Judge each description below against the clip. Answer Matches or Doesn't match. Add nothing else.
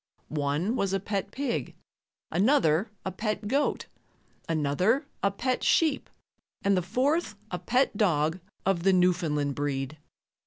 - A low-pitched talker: Doesn't match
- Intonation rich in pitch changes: Matches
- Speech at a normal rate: Doesn't match